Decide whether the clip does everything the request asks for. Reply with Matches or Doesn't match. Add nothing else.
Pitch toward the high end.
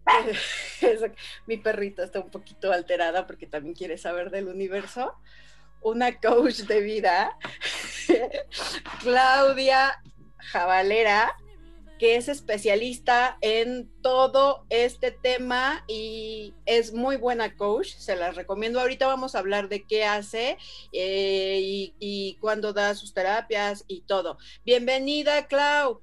Matches